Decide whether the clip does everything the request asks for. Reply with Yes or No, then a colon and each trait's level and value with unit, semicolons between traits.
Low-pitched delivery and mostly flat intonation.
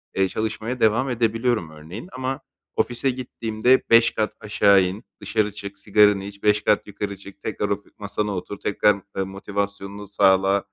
Yes: low, 105 Hz; narrow, 2.1 semitones